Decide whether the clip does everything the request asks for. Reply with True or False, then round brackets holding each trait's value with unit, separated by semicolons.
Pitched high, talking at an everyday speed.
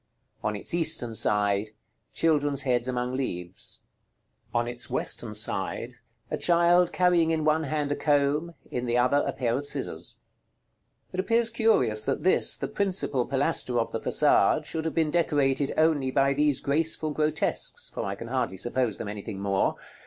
False (140 Hz; 165 wpm)